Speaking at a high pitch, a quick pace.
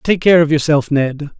No: medium, 150 Hz; fast, 215 wpm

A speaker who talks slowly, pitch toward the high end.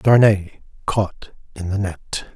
No: slow, 125 wpm; low, 100 Hz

